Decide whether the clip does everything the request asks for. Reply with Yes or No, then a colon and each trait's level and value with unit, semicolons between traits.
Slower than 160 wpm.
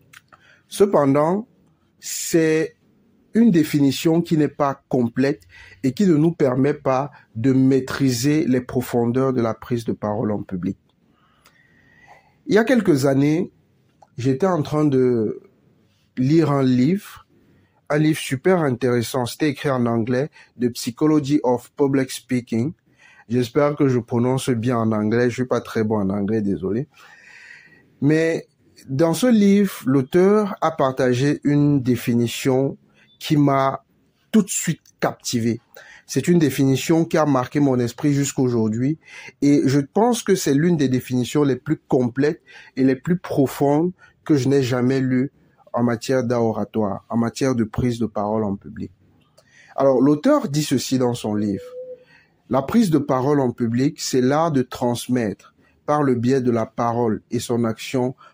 Yes: average, 150 wpm